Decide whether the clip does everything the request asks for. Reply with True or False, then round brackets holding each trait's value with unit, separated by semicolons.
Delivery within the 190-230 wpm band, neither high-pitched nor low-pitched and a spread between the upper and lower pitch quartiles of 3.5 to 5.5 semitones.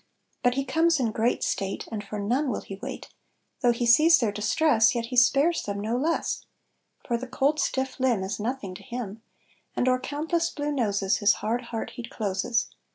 False (195 wpm; 240 Hz; 4.3 semitones)